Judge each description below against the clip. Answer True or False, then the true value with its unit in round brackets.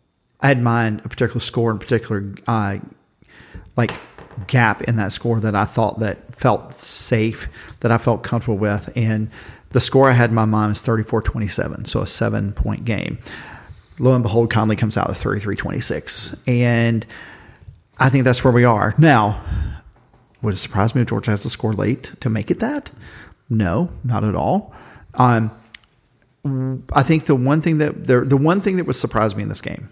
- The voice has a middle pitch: False (115 Hz)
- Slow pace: False (185 wpm)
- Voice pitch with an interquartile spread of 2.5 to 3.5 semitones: True (2.8 semitones)